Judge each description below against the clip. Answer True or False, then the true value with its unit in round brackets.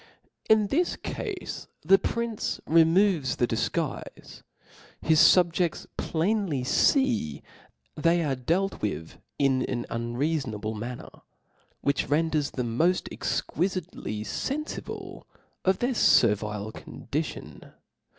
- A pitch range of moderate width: False (7.9 semitones)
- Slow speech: True (100 wpm)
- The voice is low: False (160 Hz)